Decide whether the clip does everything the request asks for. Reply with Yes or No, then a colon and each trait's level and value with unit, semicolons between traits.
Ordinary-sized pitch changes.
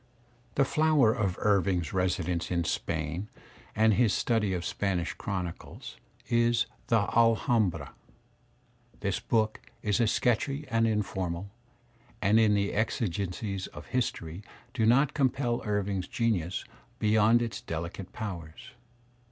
Yes: average, 4.0 semitones